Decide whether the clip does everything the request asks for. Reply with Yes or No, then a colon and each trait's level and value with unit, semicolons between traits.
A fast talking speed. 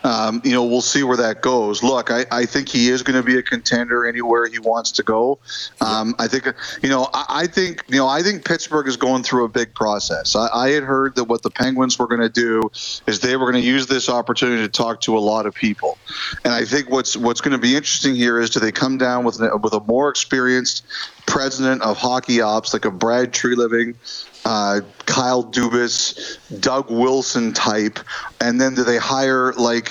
Yes: fast, 225 wpm